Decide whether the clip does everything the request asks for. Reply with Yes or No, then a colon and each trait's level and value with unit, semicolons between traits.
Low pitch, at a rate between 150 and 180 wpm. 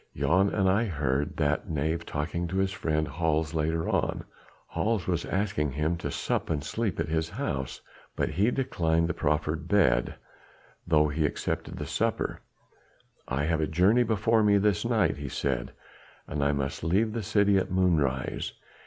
Yes: very low, 80 Hz; average, 165 wpm